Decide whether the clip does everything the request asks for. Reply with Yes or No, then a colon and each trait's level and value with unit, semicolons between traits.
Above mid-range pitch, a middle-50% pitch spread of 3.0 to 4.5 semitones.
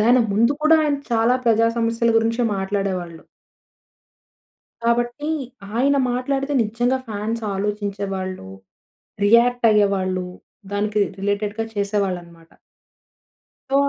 Yes: high, 215 Hz; average, 3.4 semitones